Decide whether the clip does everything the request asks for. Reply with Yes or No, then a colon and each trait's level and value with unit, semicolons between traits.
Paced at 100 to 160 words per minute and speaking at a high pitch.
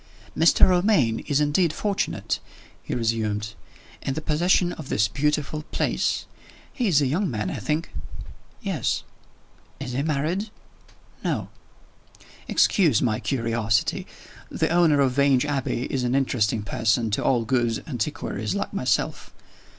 No: slow, 135 wpm; low, 135 Hz